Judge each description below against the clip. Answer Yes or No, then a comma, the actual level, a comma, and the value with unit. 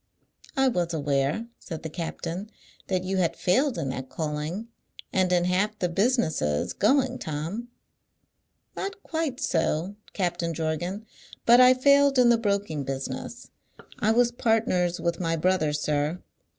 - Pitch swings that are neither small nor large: No, wide, 6.5 semitones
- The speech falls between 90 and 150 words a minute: Yes, average, 140 wpm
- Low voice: No, medium, 180 Hz